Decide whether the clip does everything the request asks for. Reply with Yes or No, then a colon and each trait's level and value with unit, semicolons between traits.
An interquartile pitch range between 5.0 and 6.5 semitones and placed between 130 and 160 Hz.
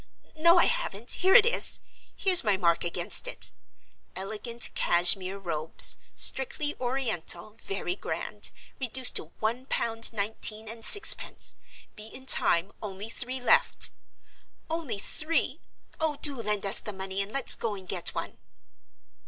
No: wide, 5.4 semitones; high, 220 Hz